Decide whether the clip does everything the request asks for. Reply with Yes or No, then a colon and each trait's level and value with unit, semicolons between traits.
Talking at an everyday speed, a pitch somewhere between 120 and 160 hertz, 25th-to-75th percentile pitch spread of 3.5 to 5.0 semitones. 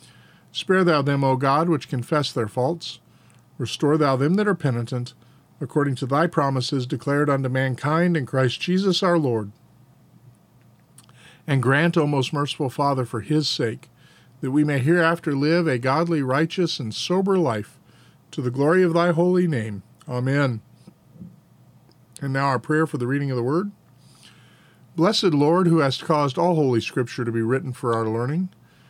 Yes: average, 165 wpm; medium, 140 Hz; average, 4.3 semitones